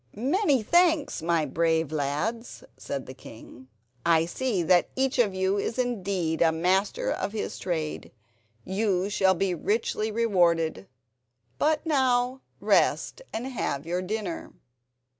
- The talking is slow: Yes, slow, 130 wpm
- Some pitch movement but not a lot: No, wide, 6.8 semitones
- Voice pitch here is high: Yes, high, 195 Hz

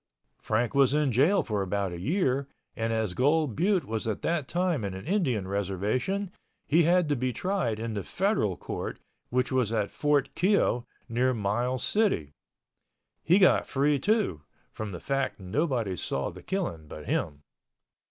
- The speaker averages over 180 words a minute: No, average, 160 wpm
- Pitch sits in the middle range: No, low, 125 Hz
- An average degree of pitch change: No, wide, 7.7 semitones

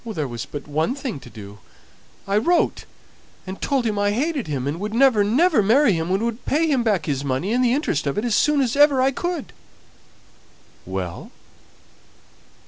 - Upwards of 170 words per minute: Yes, average, 190 wpm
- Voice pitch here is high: Yes, high, 215 Hz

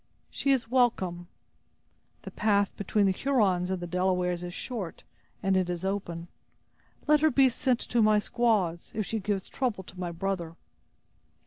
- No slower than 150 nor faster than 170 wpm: Yes, average, 160 wpm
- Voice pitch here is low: No, high, 195 Hz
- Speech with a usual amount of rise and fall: Yes, average, 4.5 semitones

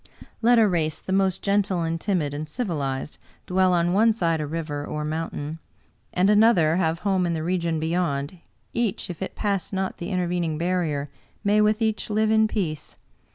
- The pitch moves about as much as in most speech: Yes, average, 4.1 semitones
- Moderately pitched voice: Yes, medium, 180 Hz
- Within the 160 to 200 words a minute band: Yes, average, 185 wpm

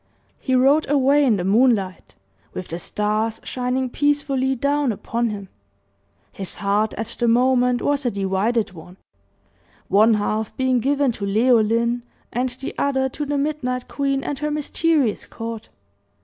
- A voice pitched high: Yes, high, 245 Hz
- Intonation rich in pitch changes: No, average, 4.2 semitones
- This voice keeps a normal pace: Yes, average, 150 wpm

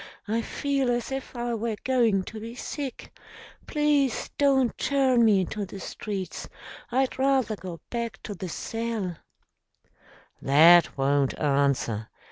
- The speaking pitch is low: No, high, 225 Hz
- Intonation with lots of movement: Yes, wide, 6.1 semitones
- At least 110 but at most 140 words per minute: Yes, slow, 135 wpm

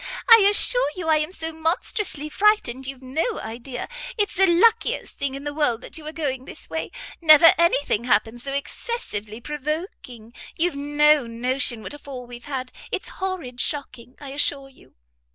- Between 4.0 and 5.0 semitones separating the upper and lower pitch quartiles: Yes, average, 4.5 semitones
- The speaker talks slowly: No, average, 175 wpm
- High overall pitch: Yes, very high, 290 Hz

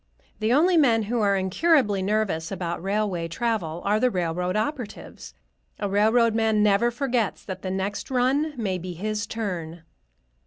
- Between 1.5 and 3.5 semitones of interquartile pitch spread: No, average, 4.0 semitones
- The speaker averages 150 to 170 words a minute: Yes, average, 155 wpm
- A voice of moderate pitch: No, high, 210 Hz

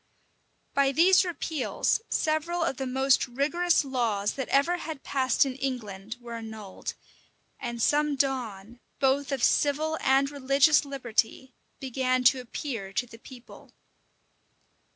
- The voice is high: Yes, very high, 265 Hz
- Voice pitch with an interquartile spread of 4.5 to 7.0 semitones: No, average, 3.1 semitones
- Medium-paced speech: No, slow, 130 wpm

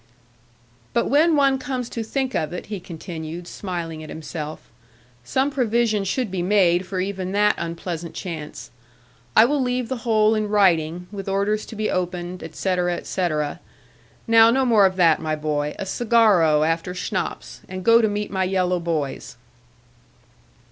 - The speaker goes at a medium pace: Yes, average, 160 wpm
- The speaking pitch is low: No, medium, 185 Hz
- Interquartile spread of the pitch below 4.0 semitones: No, average, 4.7 semitones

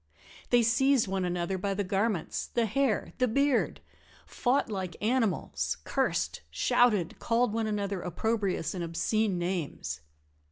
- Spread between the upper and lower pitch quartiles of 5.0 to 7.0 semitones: No, average, 4.4 semitones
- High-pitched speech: Yes, high, 205 Hz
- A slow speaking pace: Yes, slow, 130 wpm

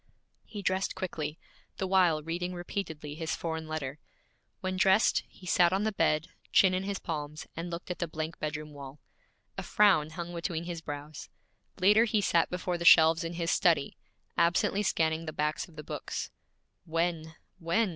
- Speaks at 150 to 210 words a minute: Yes, average, 175 wpm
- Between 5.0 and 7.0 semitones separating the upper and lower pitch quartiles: No, average, 2.8 semitones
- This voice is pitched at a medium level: Yes, medium, 170 Hz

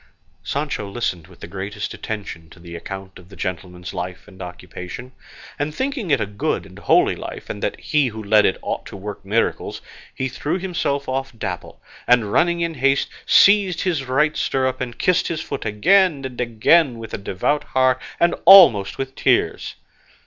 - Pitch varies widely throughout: Yes, wide, 7.3 semitones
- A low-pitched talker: Yes, low, 120 Hz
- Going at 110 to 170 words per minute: No, average, 185 wpm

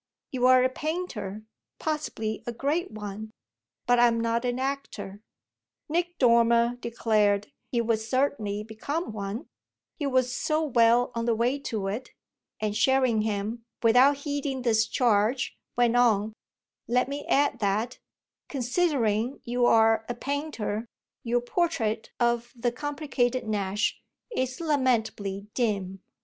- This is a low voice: No, high, 240 Hz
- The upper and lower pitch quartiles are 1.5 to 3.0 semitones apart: No, average, 3.4 semitones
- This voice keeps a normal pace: No, slow, 125 wpm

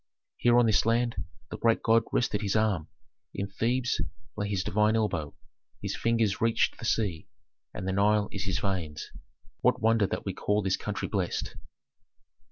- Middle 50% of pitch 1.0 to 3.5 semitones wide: Yes, average, 2.8 semitones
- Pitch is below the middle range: Yes, low, 105 Hz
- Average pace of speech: Yes, average, 170 wpm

